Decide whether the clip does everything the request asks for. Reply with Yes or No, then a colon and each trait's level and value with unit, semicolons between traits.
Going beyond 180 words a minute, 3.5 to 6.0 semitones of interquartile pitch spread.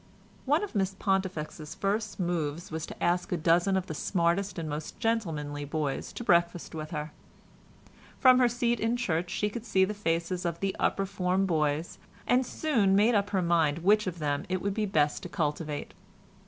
Yes: average, 190 wpm; average, 4.2 semitones